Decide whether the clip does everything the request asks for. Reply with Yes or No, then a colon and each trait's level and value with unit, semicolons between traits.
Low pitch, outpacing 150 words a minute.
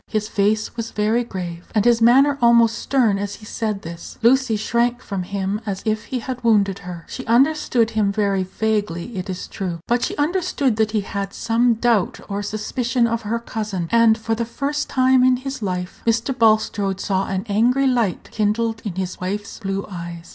No: high, 220 Hz; average, 190 wpm